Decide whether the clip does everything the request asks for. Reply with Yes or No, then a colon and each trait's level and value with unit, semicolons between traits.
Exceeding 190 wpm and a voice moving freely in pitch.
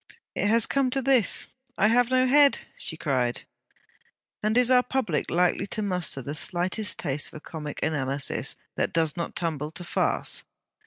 No: average, 165 wpm; wide, 8.2 semitones